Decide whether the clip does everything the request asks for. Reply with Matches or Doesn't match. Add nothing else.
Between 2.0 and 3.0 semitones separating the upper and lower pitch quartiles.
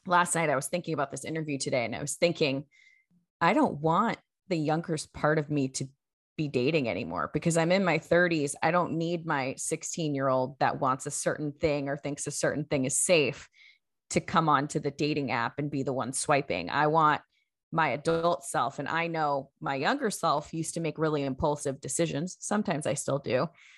Matches